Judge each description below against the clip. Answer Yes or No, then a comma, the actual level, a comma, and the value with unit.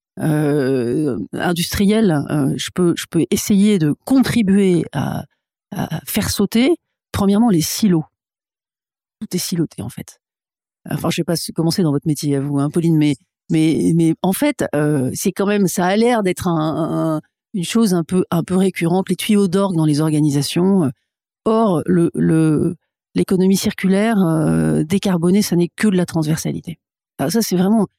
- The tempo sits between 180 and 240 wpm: No, average, 170 wpm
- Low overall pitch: No, medium, 175 Hz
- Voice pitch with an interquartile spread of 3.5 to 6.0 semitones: Yes, average, 4.1 semitones